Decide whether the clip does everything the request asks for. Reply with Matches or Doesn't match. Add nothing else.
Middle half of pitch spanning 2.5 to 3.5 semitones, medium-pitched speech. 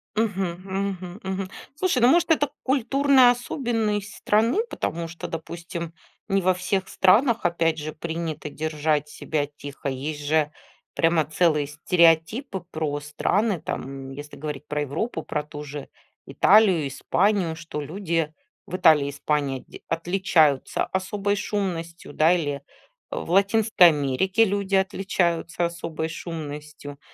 Doesn't match